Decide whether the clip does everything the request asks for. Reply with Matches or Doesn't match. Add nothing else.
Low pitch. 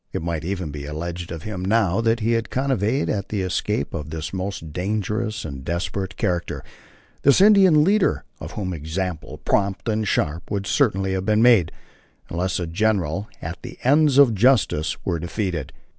Matches